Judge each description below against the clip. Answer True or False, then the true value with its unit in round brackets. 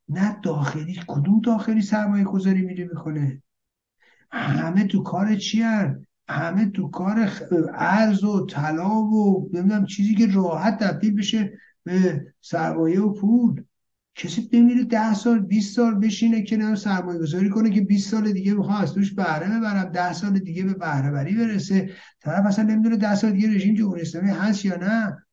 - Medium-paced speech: False (165 wpm)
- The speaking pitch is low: False (200 Hz)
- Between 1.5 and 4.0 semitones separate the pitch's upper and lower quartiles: True (3.3 semitones)